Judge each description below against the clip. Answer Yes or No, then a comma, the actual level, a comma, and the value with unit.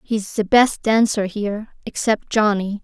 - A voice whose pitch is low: No, high, 210 Hz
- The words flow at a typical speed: Yes, average, 150 wpm